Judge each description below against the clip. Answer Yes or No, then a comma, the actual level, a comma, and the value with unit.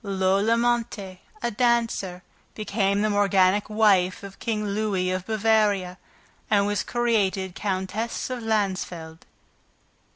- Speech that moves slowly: Yes, slow, 110 wpm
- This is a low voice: No, high, 205 Hz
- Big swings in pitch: No, average, 2.7 semitones